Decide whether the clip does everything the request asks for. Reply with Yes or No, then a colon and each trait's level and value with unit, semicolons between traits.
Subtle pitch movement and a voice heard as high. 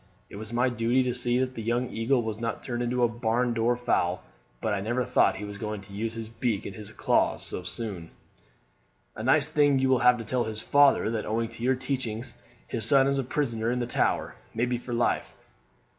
No: narrow, 2.3 semitones; low, 120 Hz